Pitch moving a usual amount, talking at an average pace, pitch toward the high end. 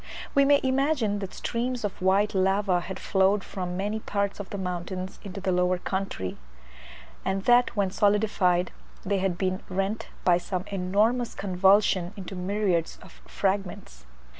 No: narrow, 2.1 semitones; average, 150 wpm; high, 195 Hz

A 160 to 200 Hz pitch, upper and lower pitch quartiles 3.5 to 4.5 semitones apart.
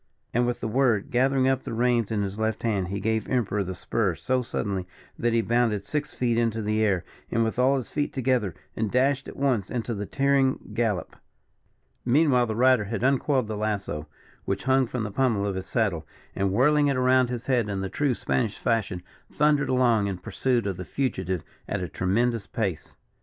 No: low, 115 Hz; average, 4.2 semitones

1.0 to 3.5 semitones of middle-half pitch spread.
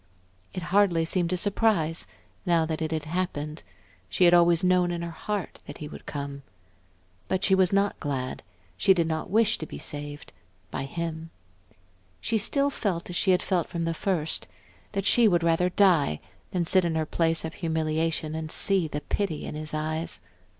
Yes: average, 2.8 semitones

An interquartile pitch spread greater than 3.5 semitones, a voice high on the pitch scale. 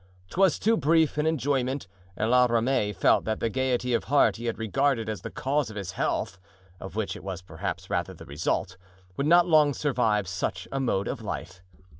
No: wide, 5.4 semitones; low, 125 Hz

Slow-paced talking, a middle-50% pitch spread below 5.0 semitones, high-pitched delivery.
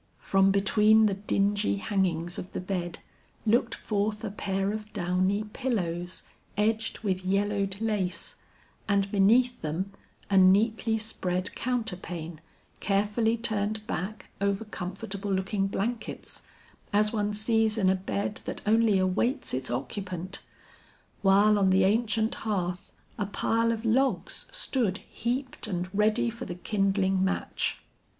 Yes: slow, 130 wpm; average, 2.7 semitones; high, 200 Hz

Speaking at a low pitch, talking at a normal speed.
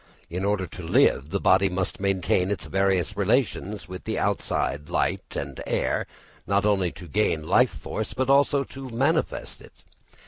Yes: very low, 95 Hz; average, 165 wpm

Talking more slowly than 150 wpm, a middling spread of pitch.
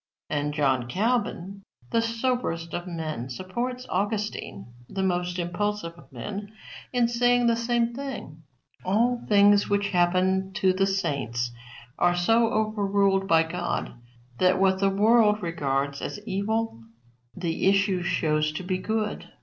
Yes: slow, 135 wpm; average, 4.4 semitones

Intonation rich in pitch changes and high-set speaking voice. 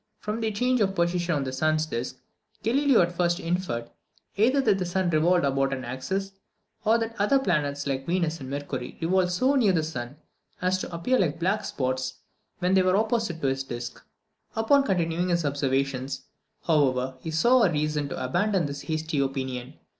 No: wide, 5.9 semitones; medium, 165 Hz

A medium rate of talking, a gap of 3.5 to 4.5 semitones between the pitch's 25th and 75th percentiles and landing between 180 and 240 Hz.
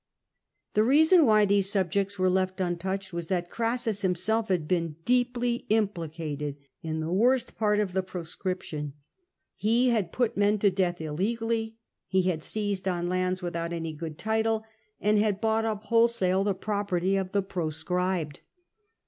Yes: average, 155 wpm; average, 3.9 semitones; high, 190 Hz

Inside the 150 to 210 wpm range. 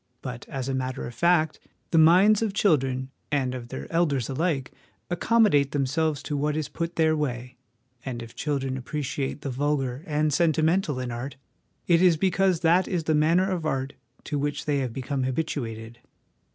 Yes: average, 180 wpm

